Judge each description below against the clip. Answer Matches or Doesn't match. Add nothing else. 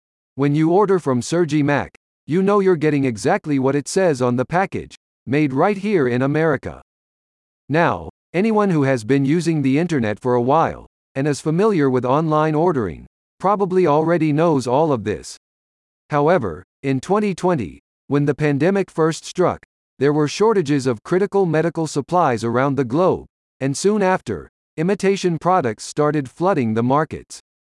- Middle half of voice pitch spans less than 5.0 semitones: Doesn't match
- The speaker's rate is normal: Matches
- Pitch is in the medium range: Matches